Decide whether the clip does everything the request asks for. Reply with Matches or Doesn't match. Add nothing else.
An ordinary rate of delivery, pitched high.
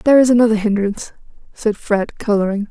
Matches